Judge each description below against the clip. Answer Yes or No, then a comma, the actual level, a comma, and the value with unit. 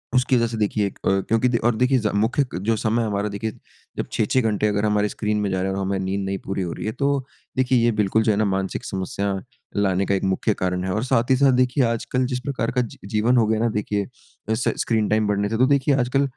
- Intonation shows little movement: No, average, 3.6 semitones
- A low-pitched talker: Yes, low, 110 Hz